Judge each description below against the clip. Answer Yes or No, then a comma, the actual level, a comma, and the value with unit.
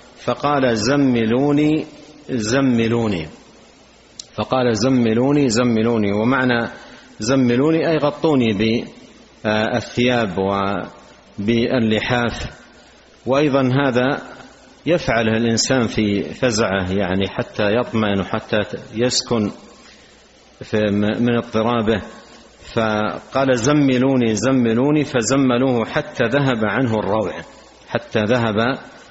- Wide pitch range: No, average, 3.2 semitones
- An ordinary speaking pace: Yes, average, 75 wpm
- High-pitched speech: No, low, 120 Hz